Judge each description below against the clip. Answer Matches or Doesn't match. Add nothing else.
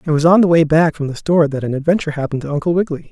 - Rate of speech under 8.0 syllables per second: Doesn't match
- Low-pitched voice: Doesn't match